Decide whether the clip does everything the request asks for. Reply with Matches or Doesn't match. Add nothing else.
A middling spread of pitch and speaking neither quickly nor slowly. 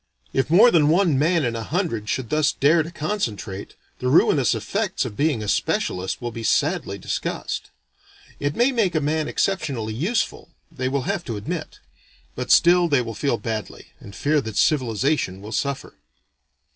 Doesn't match